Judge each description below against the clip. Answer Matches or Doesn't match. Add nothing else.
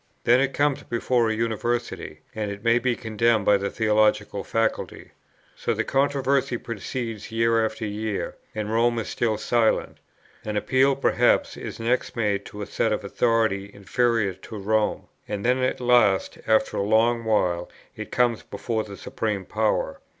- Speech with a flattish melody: Matches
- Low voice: Matches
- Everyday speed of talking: Matches